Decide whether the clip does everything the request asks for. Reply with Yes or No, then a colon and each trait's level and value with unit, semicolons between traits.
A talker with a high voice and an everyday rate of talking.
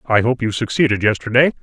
No: low, 120 Hz; average, 185 wpm